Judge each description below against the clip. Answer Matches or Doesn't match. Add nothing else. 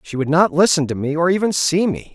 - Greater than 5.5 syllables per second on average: Matches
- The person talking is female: Doesn't match